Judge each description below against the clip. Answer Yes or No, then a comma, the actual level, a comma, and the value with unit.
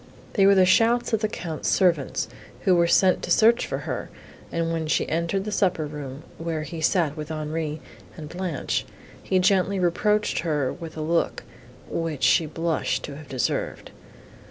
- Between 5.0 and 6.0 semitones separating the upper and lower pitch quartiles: No, average, 3.5 semitones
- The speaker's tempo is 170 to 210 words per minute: Yes, average, 175 wpm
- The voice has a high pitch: No, medium, 165 Hz